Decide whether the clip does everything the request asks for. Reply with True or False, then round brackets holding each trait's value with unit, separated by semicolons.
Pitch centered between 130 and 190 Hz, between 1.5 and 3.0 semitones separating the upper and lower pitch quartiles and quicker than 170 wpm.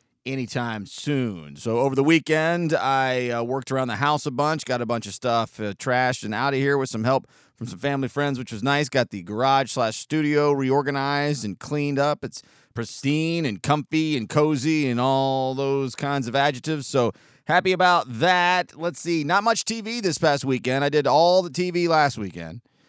False (140 Hz; 3.4 semitones; 195 wpm)